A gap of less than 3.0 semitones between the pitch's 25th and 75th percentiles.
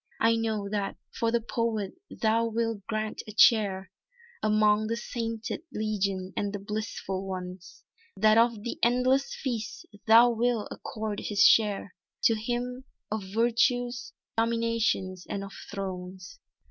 Yes: narrow, 2.4 semitones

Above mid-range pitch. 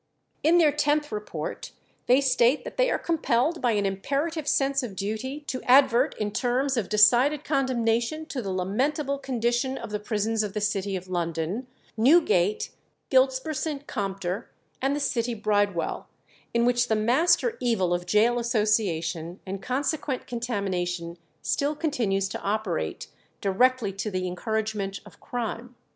Yes: high, 235 Hz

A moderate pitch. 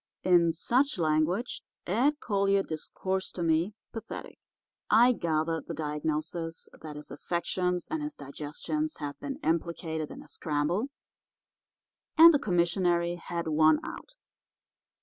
Yes: medium, 170 Hz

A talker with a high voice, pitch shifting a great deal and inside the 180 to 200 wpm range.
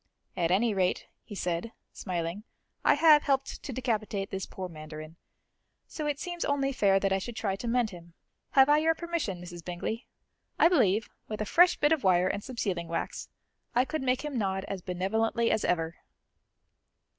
Yes: high, 210 Hz; wide, 6.8 semitones; average, 185 wpm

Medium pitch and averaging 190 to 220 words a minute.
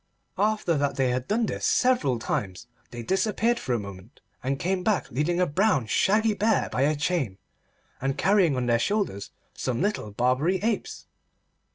No: medium, 150 Hz; average, 170 wpm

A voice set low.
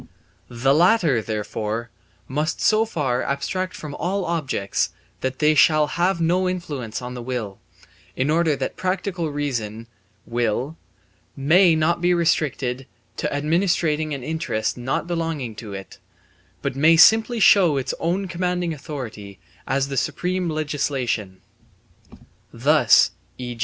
No: medium, 150 Hz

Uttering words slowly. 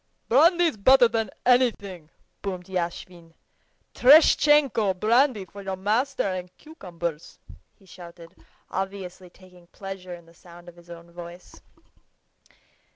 Yes: slow, 115 wpm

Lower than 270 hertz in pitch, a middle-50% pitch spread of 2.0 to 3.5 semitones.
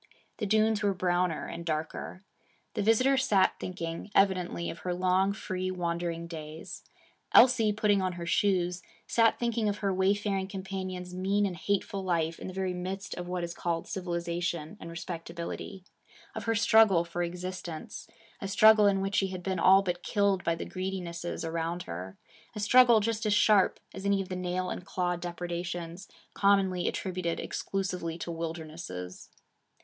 Yes: medium, 185 Hz; narrow, 2.5 semitones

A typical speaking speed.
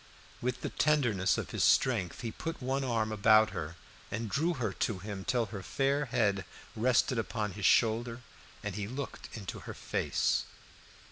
Yes: average, 165 wpm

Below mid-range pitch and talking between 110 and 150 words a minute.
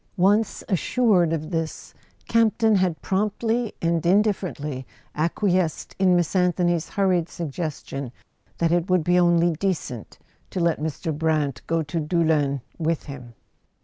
No: medium, 170 Hz; slow, 135 wpm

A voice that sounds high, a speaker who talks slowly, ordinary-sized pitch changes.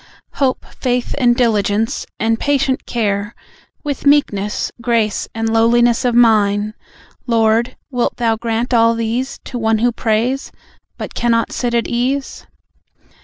No: high, 230 Hz; slow, 130 wpm; narrow, 1.7 semitones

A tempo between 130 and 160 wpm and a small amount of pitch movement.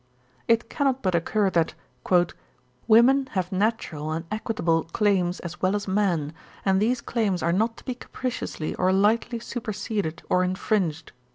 No: average, 150 wpm; average, 4.5 semitones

